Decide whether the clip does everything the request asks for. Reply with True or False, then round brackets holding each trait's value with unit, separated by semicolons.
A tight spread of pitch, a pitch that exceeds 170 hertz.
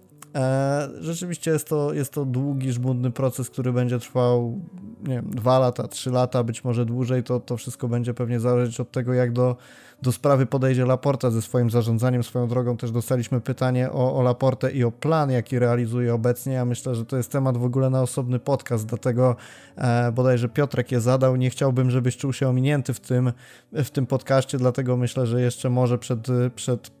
False (1.3 semitones; 125 Hz)